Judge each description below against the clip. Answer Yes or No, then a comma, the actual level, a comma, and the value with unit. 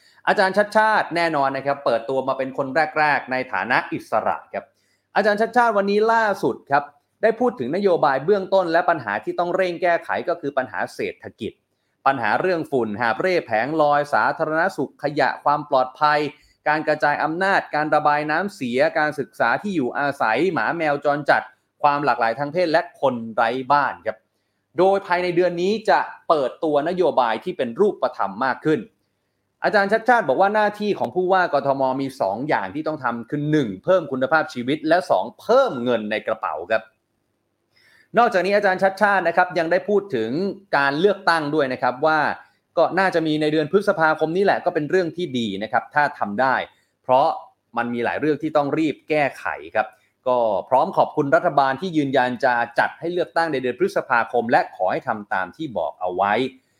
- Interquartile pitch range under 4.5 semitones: No, wide, 5.6 semitones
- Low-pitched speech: No, medium, 155 Hz